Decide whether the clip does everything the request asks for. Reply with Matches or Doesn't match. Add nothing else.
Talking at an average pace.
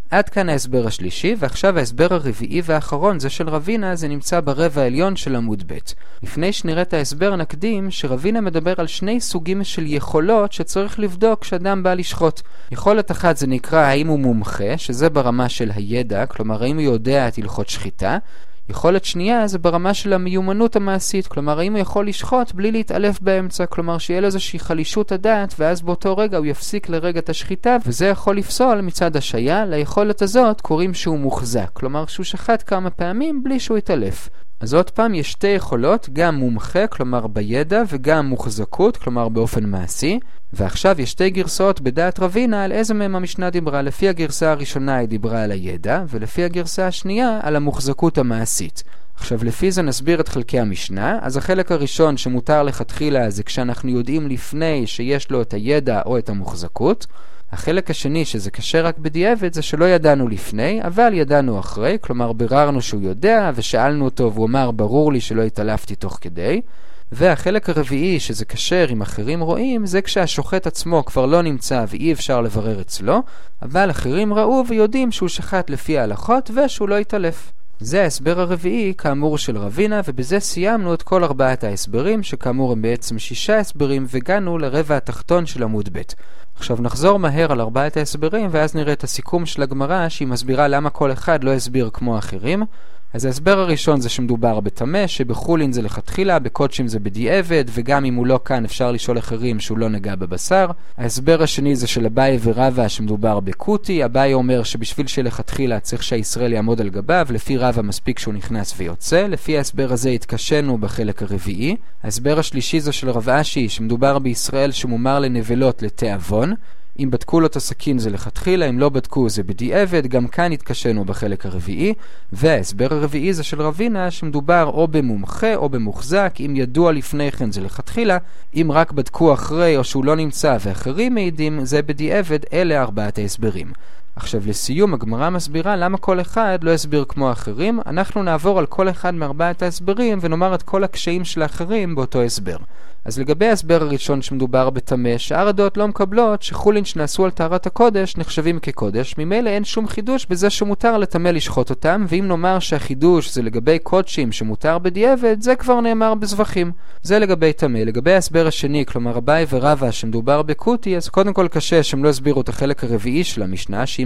Doesn't match